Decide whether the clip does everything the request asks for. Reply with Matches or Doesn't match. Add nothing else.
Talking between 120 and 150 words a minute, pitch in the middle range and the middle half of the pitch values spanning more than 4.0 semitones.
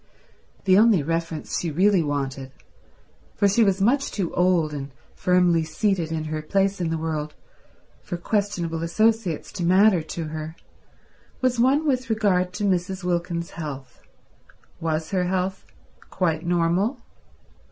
Doesn't match